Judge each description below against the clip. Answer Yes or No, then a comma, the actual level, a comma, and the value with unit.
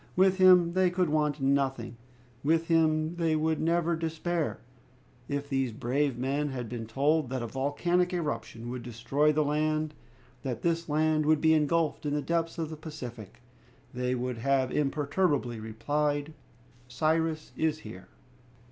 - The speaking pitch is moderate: Yes, medium, 150 Hz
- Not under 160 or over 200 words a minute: No, average, 150 wpm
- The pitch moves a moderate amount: Yes, average, 3.4 semitones